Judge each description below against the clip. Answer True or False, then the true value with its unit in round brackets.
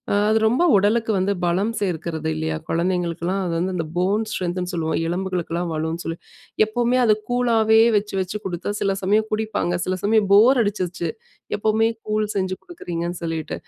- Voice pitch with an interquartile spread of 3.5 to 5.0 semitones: True (3.8 semitones)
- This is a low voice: False (190 Hz)